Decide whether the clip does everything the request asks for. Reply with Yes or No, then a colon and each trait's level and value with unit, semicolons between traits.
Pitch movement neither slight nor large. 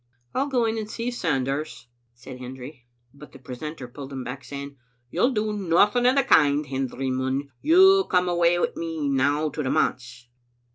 No: wide, 7.8 semitones